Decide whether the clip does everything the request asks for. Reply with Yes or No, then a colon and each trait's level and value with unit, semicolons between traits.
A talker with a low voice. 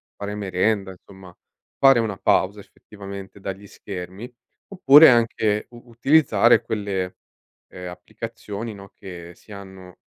Yes: low, 100 Hz